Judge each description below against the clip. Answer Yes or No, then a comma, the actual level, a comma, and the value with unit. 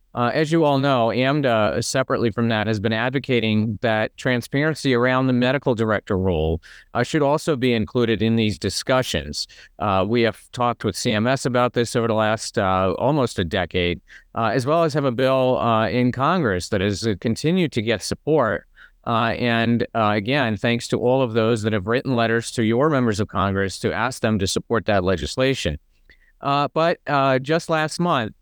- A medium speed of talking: Yes, average, 190 wpm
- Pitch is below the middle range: Yes, low, 115 Hz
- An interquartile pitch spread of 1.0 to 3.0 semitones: No, average, 3.5 semitones